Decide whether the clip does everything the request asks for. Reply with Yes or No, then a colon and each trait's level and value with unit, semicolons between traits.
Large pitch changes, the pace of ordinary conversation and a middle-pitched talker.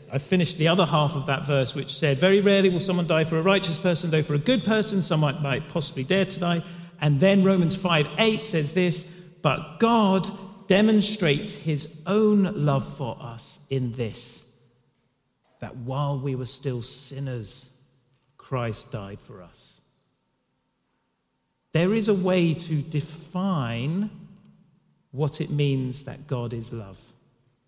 Yes: wide, 5.7 semitones; average, 150 wpm; medium, 155 Hz